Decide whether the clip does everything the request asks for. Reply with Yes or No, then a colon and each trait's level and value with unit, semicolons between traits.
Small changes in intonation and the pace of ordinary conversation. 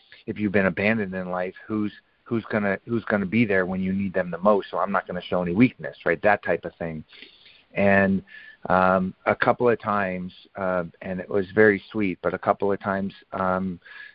No: narrow, 2.2 semitones; fast, 210 wpm